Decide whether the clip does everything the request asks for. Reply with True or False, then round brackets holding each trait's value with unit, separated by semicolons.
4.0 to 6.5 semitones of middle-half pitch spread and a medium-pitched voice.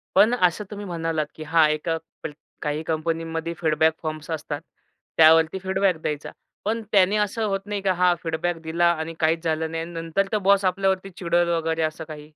False (3.0 semitones; 165 Hz)